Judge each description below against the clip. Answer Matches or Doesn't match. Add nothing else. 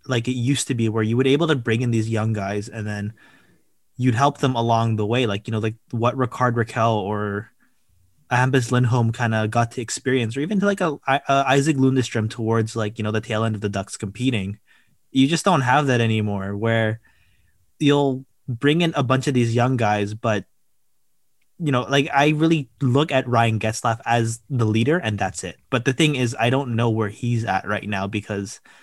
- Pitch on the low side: Matches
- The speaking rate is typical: Doesn't match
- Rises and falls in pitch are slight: Doesn't match